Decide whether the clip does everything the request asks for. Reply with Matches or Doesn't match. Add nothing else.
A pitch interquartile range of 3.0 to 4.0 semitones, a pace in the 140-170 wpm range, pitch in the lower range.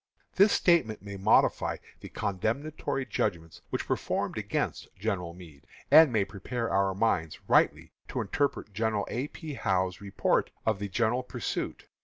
Doesn't match